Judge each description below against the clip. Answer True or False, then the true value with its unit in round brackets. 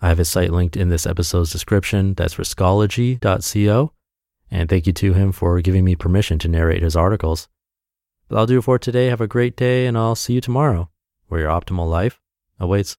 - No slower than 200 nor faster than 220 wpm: True (205 wpm)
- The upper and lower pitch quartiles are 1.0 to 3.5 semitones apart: False (4.4 semitones)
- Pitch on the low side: True (95 Hz)